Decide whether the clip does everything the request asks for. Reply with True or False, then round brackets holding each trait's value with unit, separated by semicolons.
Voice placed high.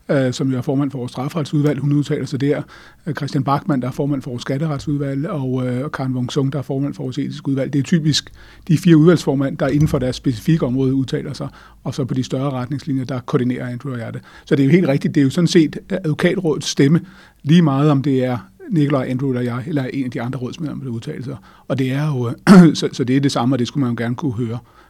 False (140 Hz)